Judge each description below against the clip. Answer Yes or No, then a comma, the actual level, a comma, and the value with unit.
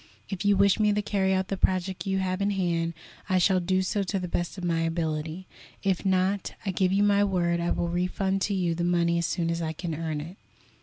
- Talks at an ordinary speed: No, fast, 245 wpm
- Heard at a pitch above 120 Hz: Yes, medium, 185 Hz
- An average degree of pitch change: No, narrow, 2.3 semitones